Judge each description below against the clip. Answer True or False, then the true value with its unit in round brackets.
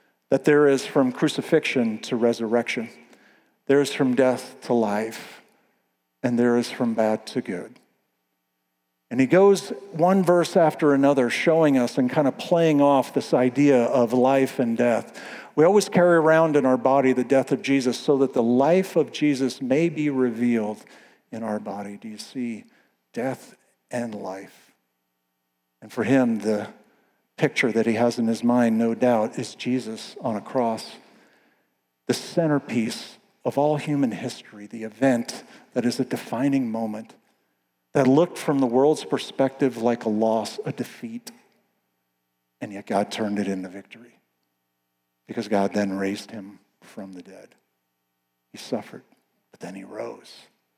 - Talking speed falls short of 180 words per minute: True (155 wpm)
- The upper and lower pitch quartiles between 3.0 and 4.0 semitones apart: False (5.1 semitones)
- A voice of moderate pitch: False (120 Hz)